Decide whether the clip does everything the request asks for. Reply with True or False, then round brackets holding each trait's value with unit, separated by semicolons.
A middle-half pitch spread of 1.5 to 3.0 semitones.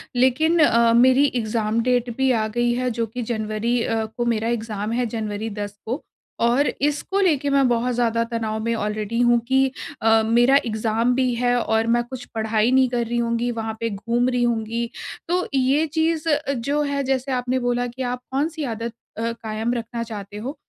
True (2.5 semitones)